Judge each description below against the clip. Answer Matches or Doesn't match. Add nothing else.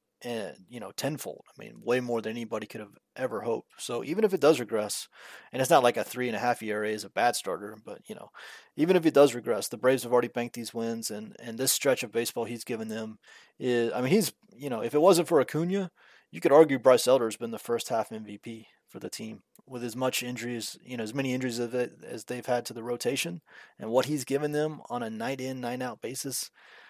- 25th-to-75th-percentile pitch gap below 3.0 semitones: Matches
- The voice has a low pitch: Matches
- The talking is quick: Matches